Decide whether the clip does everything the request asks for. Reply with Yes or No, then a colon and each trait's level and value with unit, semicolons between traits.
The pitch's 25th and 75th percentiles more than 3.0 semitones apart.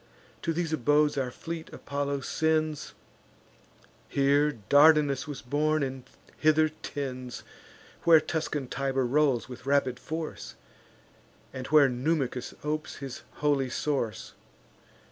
No: narrow, 2.6 semitones